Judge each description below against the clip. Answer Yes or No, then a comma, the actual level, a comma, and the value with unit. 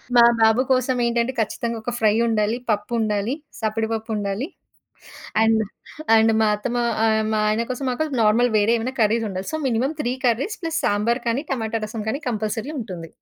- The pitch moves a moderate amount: No, narrow, 2.1 semitones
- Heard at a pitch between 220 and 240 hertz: Yes, high, 225 Hz